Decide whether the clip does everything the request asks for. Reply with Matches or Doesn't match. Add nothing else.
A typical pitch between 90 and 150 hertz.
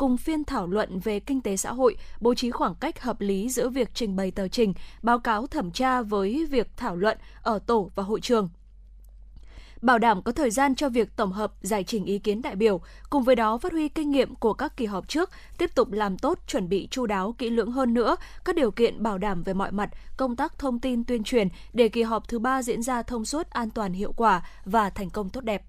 Doesn't match